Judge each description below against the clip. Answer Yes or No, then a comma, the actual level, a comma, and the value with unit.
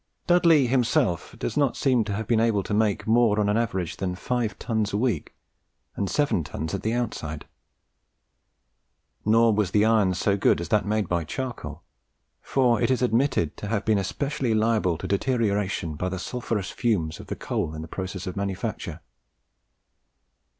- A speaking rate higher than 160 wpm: Yes, average, 175 wpm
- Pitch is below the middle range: Yes, low, 105 Hz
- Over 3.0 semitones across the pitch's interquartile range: Yes, average, 4.1 semitones